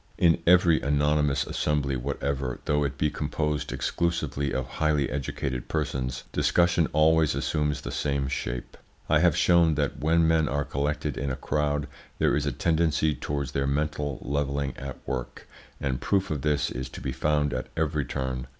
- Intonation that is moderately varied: No, narrow, 2.0 semitones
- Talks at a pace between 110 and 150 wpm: No, average, 170 wpm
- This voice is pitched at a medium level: No, very low, 75 Hz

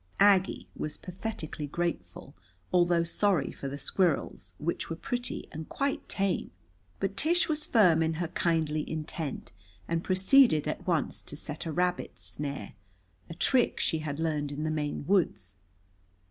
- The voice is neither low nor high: Yes, medium, 165 Hz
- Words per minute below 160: Yes, average, 150 wpm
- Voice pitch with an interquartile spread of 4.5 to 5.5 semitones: No, average, 3.9 semitones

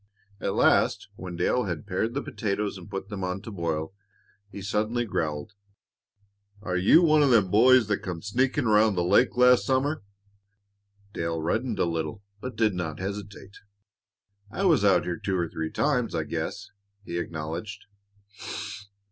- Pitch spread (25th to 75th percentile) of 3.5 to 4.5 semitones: No, average, 5.2 semitones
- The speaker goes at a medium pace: Yes, average, 160 wpm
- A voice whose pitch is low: Yes, low, 100 Hz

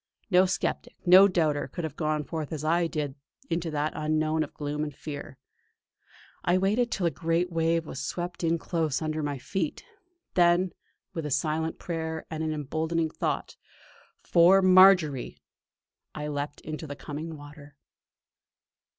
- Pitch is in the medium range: Yes, medium, 160 Hz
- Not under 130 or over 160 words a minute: Yes, average, 155 wpm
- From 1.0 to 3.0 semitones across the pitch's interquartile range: Yes, narrow, 2.5 semitones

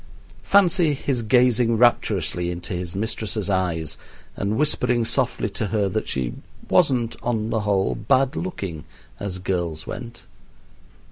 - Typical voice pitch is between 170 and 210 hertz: No, low, 110 Hz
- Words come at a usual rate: No, slow, 130 wpm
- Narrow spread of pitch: No, average, 4.9 semitones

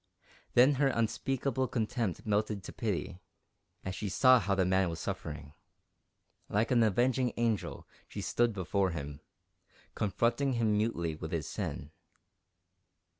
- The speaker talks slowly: Yes, slow, 130 wpm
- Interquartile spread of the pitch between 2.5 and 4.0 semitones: No, average, 4.6 semitones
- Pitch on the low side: Yes, low, 105 Hz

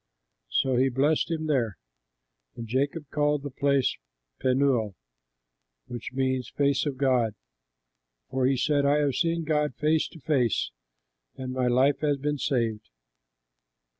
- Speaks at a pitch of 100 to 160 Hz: Yes, low, 135 Hz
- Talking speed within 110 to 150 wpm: Yes, slow, 135 wpm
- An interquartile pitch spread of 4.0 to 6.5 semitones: No, narrow, 2.6 semitones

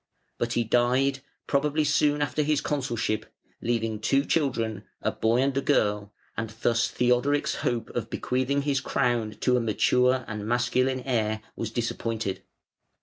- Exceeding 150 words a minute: No, average, 145 wpm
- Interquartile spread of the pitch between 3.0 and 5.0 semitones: Yes, average, 3.5 semitones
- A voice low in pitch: Yes, low, 120 Hz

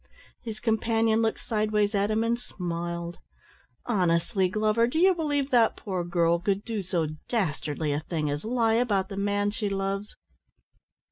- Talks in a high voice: Yes, high, 205 Hz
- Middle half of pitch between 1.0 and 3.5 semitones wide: No, average, 4.3 semitones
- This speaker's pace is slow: No, average, 155 wpm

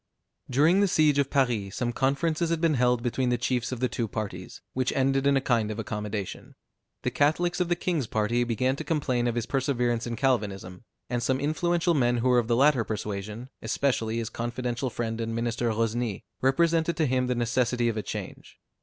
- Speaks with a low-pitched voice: Yes, low, 125 Hz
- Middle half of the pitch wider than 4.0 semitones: No, average, 3.3 semitones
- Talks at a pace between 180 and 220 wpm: Yes, average, 200 wpm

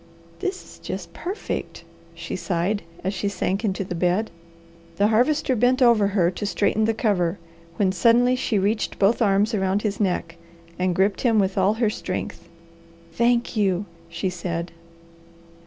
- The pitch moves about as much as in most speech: Yes, average, 3.4 semitones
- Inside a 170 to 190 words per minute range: No, average, 155 wpm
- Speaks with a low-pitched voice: No, high, 200 Hz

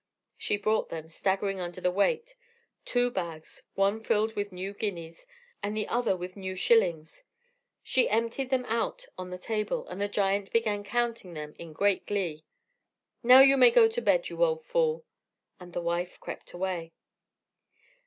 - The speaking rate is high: No, average, 165 wpm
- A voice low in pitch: No, high, 205 Hz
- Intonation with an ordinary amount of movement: Yes, average, 4.9 semitones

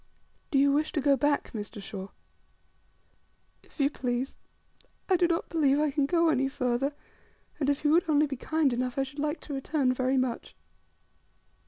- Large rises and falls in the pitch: No, average, 2.8 semitones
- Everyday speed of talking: Yes, average, 180 wpm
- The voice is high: Yes, very high, 280 Hz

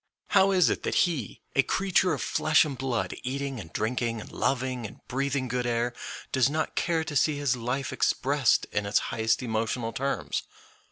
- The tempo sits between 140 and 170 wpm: No, average, 180 wpm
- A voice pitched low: Yes, low, 130 Hz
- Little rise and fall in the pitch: No, average, 3.5 semitones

